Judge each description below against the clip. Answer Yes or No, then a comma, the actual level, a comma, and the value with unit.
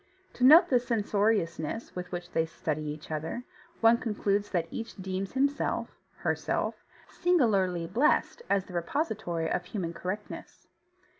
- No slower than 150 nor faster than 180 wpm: No, slow, 135 wpm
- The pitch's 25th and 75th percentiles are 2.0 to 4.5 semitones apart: No, average, 5.2 semitones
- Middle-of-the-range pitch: No, high, 195 Hz